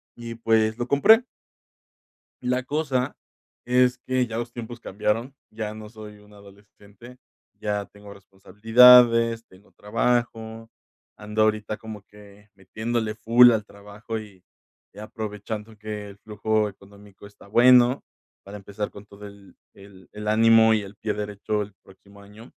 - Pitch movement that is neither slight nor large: No, narrow, 2.1 semitones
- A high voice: No, low, 110 Hz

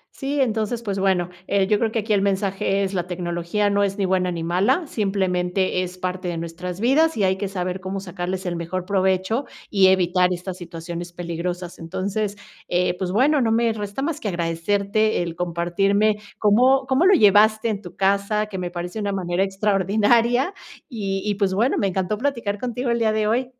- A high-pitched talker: Yes, high, 195 Hz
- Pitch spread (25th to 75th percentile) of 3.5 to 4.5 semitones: No, average, 3.1 semitones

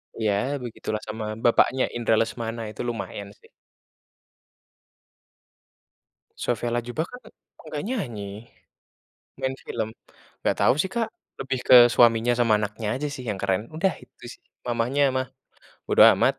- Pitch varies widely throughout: No, average, 3.4 semitones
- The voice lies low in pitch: Yes, low, 120 Hz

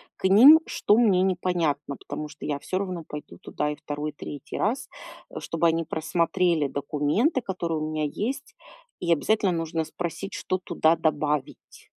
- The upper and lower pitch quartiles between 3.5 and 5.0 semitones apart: Yes, average, 3.8 semitones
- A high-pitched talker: No, medium, 165 Hz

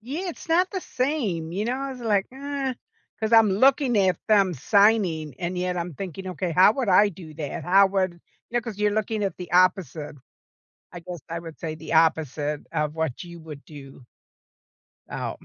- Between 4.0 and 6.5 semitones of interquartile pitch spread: Yes, average, 5.2 semitones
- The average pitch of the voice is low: No, medium, 185 Hz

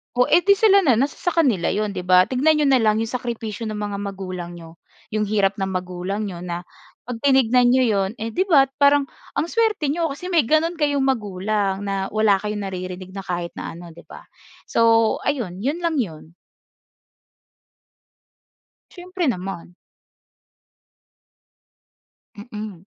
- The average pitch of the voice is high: Yes, high, 215 Hz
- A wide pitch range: Yes, wide, 6.6 semitones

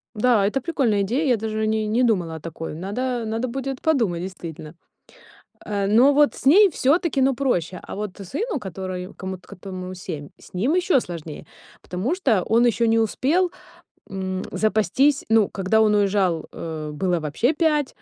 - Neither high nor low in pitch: No, high, 215 Hz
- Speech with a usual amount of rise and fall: No, wide, 6.0 semitones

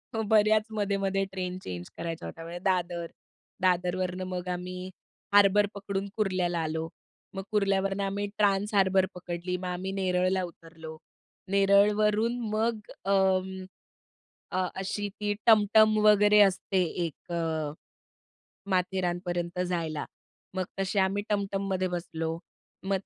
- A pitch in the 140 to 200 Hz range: Yes, high, 190 Hz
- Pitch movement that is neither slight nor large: No, narrow, 2.1 semitones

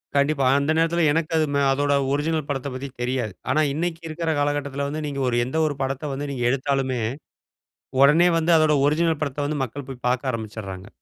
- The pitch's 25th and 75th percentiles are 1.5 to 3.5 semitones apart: Yes, average, 2.8 semitones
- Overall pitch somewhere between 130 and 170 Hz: Yes, medium, 140 Hz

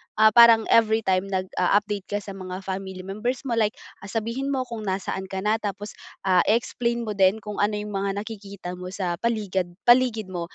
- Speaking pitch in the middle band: No, high, 205 Hz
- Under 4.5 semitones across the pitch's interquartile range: Yes, average, 2.8 semitones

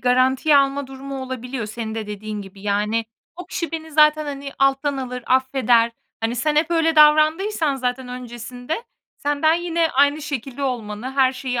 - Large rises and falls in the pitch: No, average, 3.7 semitones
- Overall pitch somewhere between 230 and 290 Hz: Yes, very high, 265 Hz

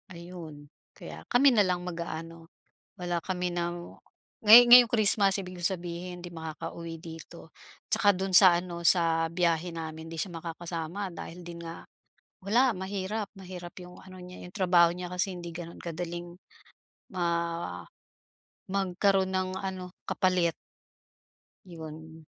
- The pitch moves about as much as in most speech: No, narrow, 1.9 semitones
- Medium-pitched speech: Yes, medium, 175 Hz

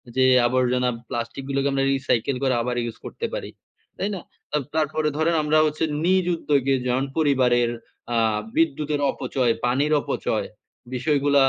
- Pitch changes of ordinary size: Yes, average, 3.2 semitones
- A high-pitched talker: No, medium, 140 Hz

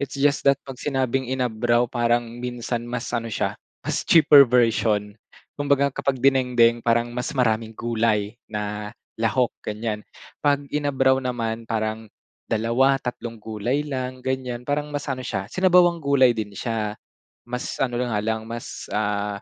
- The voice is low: Yes, low, 120 Hz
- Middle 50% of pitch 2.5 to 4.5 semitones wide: Yes, average, 2.9 semitones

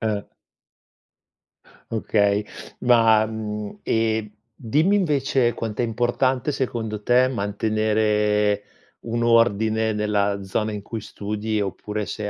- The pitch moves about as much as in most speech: No, narrow, 1.9 semitones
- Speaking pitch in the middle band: No, low, 110 Hz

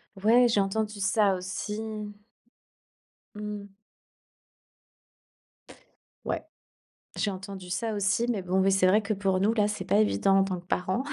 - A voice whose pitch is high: Yes, high, 200 Hz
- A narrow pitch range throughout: Yes, narrow, 1.9 semitones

